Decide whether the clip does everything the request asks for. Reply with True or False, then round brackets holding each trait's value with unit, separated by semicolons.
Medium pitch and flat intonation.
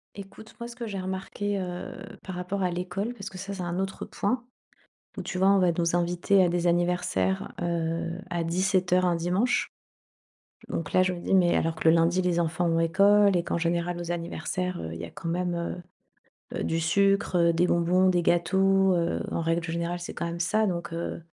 True (175 Hz; 2.0 semitones)